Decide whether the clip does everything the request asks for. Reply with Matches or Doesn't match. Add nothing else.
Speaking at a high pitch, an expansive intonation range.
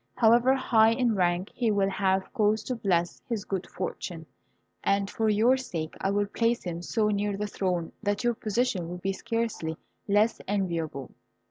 Doesn't match